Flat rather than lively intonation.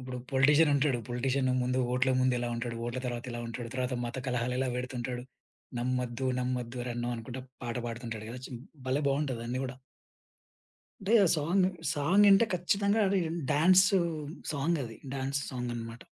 No: average, 3.2 semitones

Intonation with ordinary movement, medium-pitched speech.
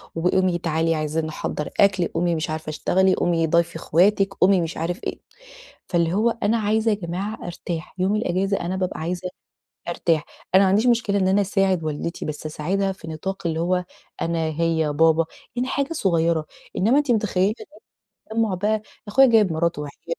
Yes: average, 3.5 semitones; medium, 180 Hz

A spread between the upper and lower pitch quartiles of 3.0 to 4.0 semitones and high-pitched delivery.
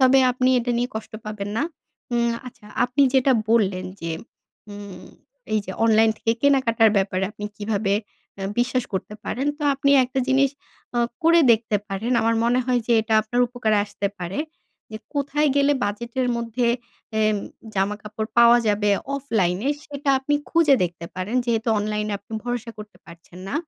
Yes: average, 3.6 semitones; high, 230 Hz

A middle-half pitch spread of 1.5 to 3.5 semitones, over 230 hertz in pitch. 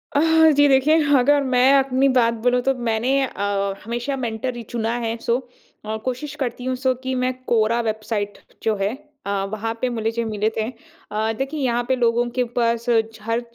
Yes: average, 2.8 semitones; high, 240 Hz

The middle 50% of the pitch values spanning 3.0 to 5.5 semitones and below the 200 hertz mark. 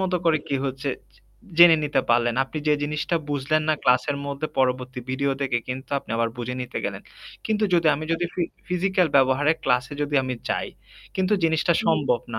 Yes: average, 4.0 semitones; medium, 140 Hz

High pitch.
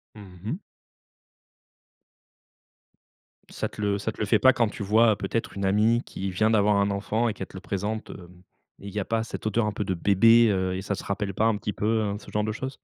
No: low, 105 Hz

